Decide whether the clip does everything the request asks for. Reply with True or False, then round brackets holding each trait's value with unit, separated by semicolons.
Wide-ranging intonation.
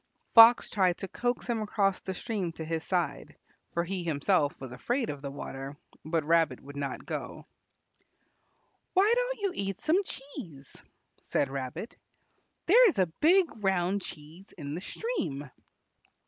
True (8.2 semitones)